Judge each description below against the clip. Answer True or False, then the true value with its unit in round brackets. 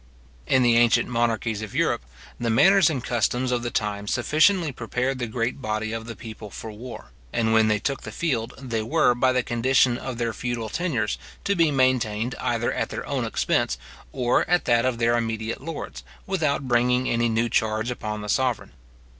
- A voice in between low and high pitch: False (120 Hz)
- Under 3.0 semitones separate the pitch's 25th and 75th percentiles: True (2.5 semitones)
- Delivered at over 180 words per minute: True (190 wpm)